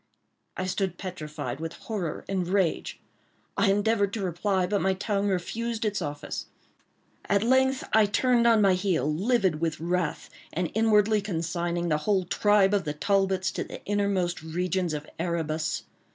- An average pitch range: Yes, average, 3.4 semitones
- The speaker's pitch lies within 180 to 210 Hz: Yes, high, 190 Hz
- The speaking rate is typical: Yes, average, 155 wpm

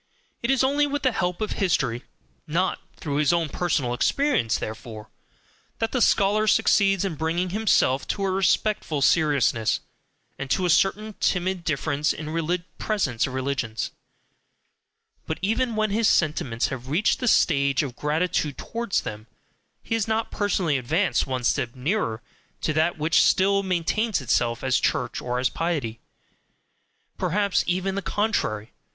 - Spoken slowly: No, average, 150 wpm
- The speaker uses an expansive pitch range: Yes, wide, 7.1 semitones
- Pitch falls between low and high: Yes, medium, 170 Hz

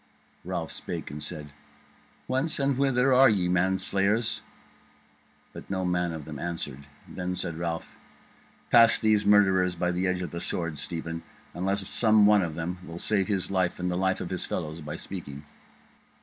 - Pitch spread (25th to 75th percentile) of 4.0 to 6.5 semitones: No, average, 3.4 semitones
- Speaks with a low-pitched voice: Yes, very low, 90 Hz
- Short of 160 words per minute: No, average, 175 wpm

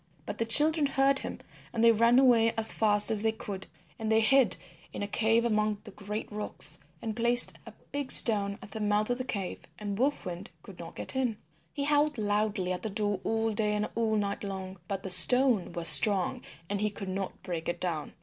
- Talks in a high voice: Yes, high, 215 Hz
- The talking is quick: Yes, fast, 215 wpm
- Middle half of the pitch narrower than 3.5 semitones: Yes, narrow, 2.6 semitones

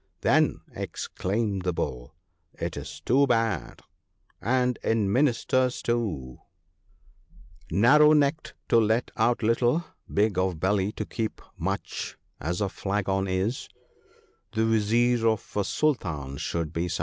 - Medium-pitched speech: No, low, 110 Hz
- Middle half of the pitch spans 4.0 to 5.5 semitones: Yes, average, 4.4 semitones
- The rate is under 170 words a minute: Yes, average, 140 wpm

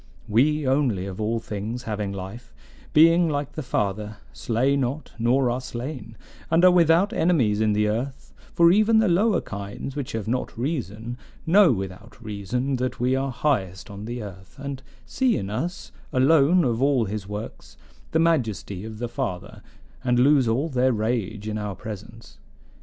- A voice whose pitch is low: Yes, low, 125 Hz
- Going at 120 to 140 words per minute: No, average, 170 wpm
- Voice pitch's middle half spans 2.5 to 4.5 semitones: No, average, 5.2 semitones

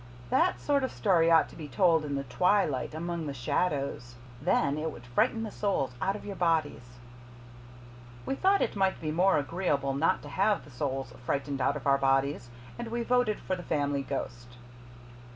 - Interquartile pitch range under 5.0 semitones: No, wide, 5.6 semitones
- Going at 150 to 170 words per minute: No, average, 190 wpm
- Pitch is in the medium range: Yes, medium, 155 Hz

